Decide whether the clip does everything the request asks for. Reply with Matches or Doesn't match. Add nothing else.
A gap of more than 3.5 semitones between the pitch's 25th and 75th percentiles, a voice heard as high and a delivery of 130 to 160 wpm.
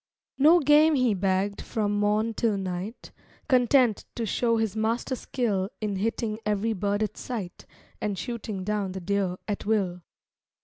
Doesn't match